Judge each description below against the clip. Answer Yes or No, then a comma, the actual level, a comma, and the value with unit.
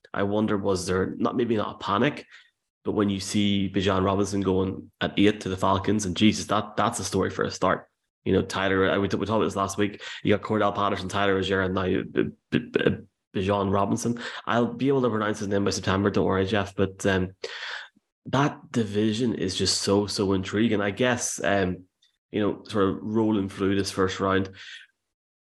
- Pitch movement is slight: Yes, narrow, 1.7 semitones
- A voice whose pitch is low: Yes, low, 100 Hz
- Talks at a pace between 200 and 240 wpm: Yes, fast, 205 wpm